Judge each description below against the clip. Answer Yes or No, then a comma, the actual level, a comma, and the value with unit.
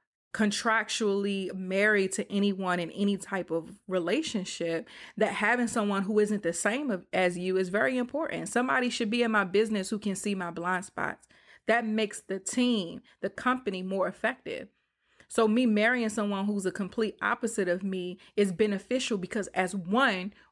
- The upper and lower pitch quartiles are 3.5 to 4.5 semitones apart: No, average, 2.9 semitones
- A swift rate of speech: No, average, 165 wpm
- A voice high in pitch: Yes, high, 205 Hz